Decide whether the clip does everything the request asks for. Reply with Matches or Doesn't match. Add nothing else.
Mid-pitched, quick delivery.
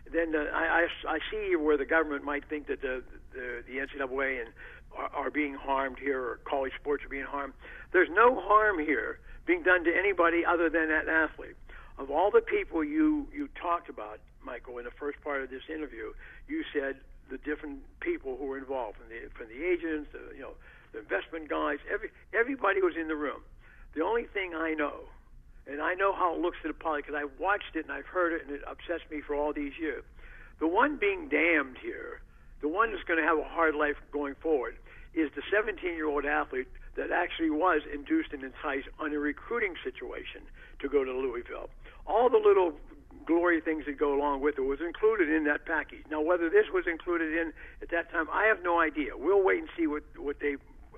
Matches